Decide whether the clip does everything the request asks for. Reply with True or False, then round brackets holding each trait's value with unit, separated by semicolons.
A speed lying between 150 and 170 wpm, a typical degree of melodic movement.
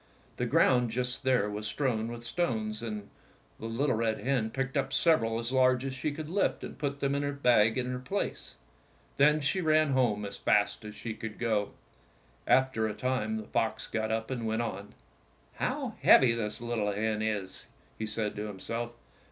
False (195 wpm; 3.3 semitones)